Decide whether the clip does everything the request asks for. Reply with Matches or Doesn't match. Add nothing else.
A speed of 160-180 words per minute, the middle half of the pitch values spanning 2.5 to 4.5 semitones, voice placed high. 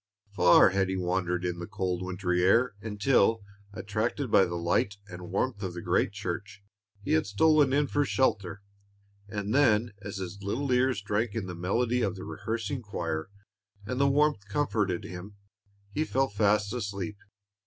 Doesn't match